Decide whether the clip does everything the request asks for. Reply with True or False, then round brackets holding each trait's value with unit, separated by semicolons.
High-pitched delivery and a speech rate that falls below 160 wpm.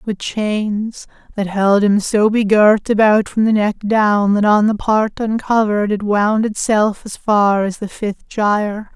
False (210 Hz; 175 wpm)